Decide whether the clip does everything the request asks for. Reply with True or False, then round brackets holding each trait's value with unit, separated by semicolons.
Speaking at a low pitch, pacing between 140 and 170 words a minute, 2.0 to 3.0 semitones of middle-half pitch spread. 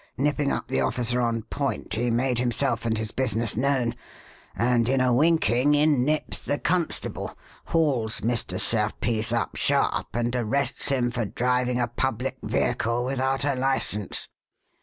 True (125 Hz; 150 wpm; 2.6 semitones)